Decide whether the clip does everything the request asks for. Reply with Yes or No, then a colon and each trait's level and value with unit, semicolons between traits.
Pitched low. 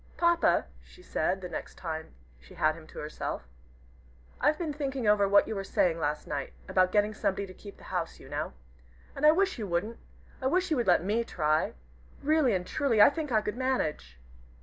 No: high, 205 Hz